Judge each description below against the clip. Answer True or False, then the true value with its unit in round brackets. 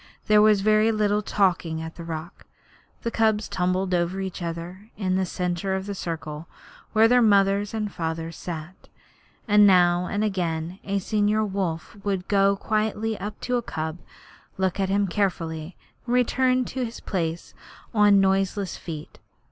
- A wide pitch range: False (3.3 semitones)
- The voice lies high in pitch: True (195 Hz)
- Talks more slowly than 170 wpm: True (160 wpm)